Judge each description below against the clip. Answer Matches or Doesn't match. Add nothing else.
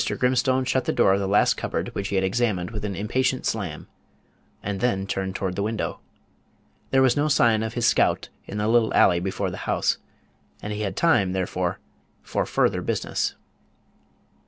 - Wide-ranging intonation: Doesn't match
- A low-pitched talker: Matches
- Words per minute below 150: Doesn't match